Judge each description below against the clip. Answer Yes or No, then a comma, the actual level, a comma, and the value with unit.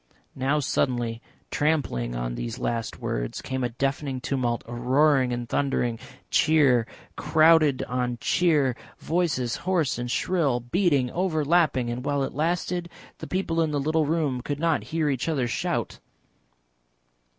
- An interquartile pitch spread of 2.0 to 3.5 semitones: No, average, 4.5 semitones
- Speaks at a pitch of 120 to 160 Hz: Yes, low, 135 Hz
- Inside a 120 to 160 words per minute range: Yes, average, 140 wpm